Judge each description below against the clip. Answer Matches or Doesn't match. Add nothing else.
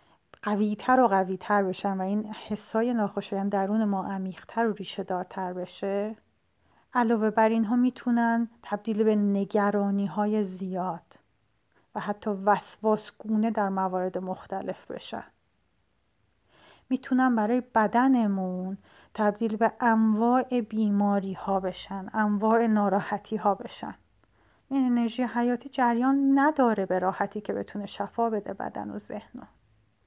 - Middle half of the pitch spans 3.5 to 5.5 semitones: Doesn't match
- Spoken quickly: Doesn't match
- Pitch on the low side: Doesn't match